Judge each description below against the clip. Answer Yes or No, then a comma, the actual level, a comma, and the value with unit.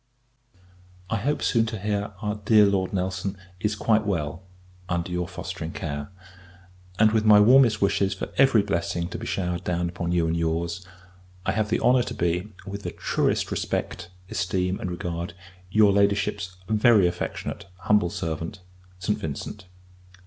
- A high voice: No, very low, 95 Hz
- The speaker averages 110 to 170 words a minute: Yes, average, 155 wpm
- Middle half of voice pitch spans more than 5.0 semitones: No, average, 3.4 semitones